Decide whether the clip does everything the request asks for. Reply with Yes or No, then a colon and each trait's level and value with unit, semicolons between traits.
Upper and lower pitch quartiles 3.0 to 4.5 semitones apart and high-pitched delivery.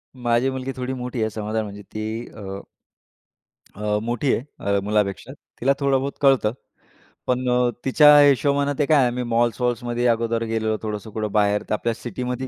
No: average, 3.3 semitones; low, 120 Hz